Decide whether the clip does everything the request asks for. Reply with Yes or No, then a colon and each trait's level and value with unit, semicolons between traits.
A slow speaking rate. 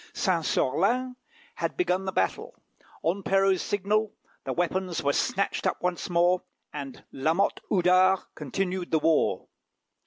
Yes: slow, 130 wpm